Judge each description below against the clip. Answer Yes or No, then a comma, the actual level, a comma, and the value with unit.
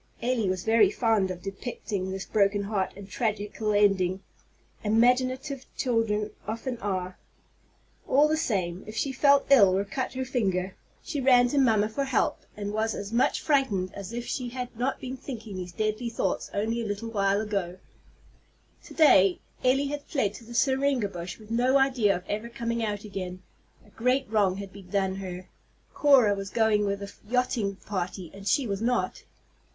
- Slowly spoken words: No, average, 175 wpm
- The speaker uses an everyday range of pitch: Yes, average, 4.1 semitones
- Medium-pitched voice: No, high, 215 Hz